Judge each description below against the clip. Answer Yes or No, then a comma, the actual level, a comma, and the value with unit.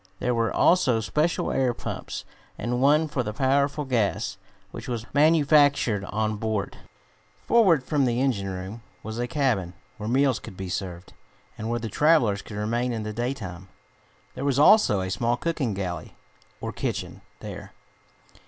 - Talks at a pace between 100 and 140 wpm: No, average, 160 wpm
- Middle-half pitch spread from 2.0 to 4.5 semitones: No, average, 5.1 semitones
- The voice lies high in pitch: No, low, 120 Hz